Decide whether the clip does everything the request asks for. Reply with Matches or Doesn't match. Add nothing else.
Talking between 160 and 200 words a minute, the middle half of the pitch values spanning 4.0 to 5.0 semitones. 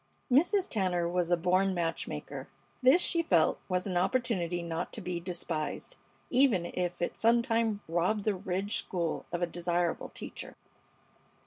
Doesn't match